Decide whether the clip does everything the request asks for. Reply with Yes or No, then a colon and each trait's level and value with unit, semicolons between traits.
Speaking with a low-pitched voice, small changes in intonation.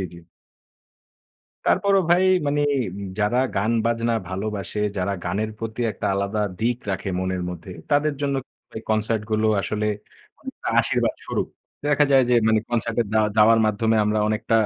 Yes: low, 110 Hz; narrow, 2.3 semitones